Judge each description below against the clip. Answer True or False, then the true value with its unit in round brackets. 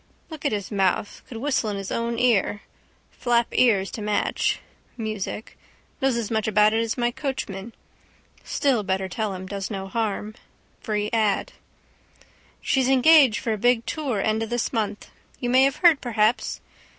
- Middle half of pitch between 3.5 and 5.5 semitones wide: False (3.0 semitones)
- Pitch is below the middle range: False (220 Hz)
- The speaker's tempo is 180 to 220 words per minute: False (165 wpm)